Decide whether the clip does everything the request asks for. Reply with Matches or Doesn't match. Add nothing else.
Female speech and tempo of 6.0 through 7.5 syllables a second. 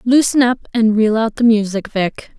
Doesn't match